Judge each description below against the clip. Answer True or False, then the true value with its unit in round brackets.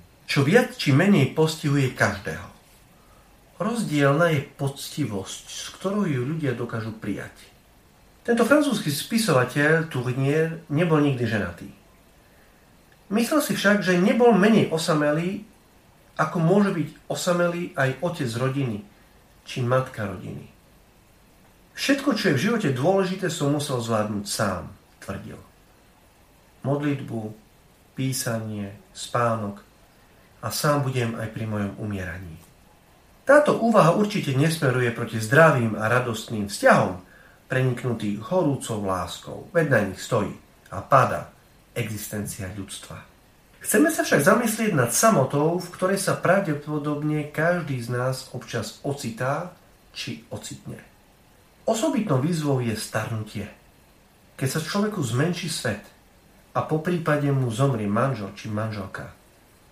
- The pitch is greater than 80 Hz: True (140 Hz)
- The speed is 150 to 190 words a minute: False (115 wpm)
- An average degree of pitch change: False (7.5 semitones)